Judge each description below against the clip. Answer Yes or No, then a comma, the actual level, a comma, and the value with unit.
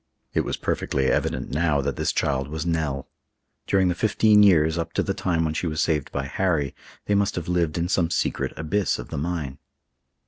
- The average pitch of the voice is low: Yes, very low, 80 Hz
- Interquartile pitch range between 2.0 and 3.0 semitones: No, average, 3.5 semitones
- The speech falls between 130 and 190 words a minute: No, fast, 205 wpm